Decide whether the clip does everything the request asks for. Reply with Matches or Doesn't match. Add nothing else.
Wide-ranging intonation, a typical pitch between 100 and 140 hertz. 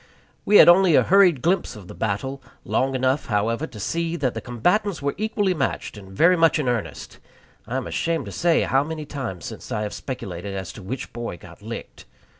Matches